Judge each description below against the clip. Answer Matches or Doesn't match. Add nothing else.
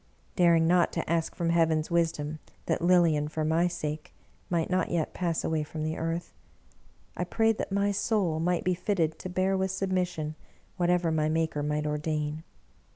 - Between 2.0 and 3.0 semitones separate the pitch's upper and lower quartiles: Matches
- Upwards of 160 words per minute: Matches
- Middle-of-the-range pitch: Matches